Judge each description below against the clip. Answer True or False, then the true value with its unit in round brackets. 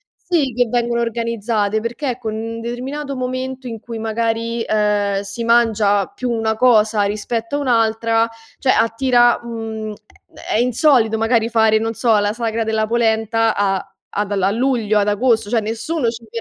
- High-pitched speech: True (225 Hz)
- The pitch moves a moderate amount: False (1.7 semitones)